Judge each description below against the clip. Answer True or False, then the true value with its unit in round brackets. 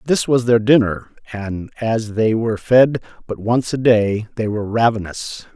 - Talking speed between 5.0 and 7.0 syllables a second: False (4.5 syllables/s)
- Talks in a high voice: False (115 Hz)